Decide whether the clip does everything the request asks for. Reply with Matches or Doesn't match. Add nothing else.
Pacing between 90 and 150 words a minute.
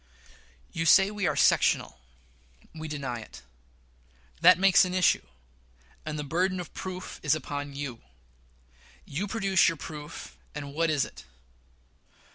Matches